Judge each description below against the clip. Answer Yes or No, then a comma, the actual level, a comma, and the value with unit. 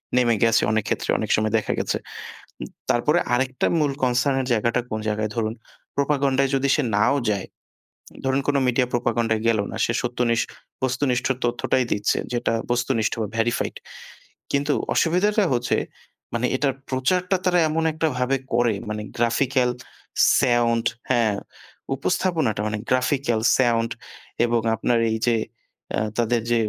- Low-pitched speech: Yes, low, 125 Hz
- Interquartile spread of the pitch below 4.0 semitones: Yes, average, 2.9 semitones